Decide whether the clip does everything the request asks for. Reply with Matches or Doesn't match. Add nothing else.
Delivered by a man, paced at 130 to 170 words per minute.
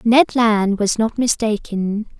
Doesn't match